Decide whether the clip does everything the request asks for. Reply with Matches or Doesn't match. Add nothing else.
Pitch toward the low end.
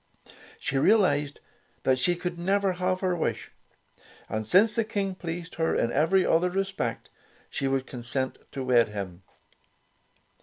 Doesn't match